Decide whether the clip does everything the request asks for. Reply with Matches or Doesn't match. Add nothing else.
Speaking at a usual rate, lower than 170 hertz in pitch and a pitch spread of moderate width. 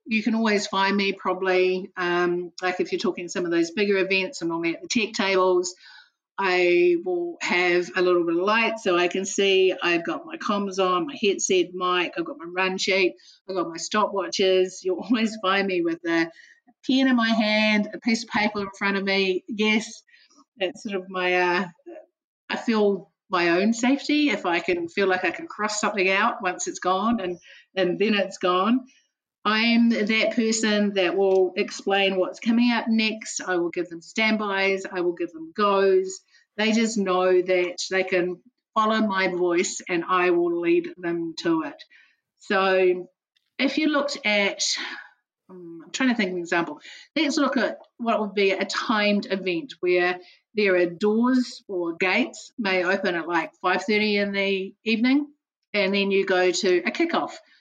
Doesn't match